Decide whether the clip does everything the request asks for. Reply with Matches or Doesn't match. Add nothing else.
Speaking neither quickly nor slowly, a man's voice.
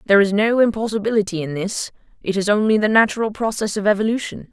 Doesn't match